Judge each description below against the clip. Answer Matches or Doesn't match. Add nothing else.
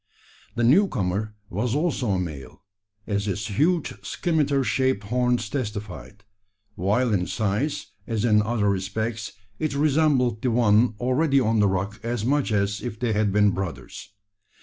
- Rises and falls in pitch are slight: Doesn't match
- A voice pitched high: Doesn't match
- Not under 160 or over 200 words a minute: Doesn't match